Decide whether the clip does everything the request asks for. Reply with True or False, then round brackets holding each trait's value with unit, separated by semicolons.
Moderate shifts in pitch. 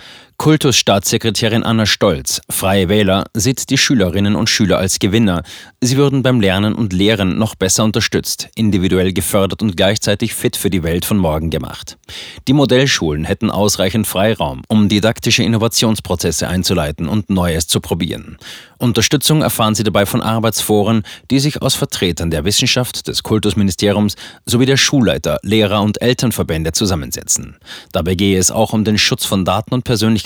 True (3.4 semitones)